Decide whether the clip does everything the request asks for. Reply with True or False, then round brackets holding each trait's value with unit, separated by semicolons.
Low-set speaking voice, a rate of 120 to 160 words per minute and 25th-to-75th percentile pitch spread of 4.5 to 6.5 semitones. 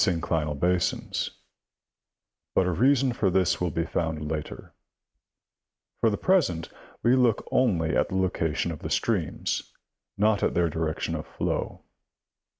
True (90 Hz; 140 wpm; 5.1 semitones)